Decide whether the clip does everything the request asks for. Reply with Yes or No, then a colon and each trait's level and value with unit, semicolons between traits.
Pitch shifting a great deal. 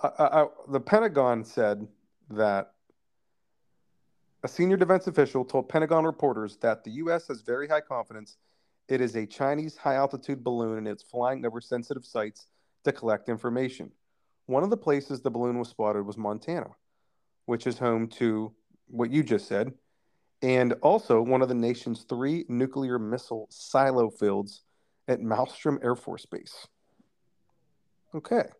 No: average, 3.7 semitones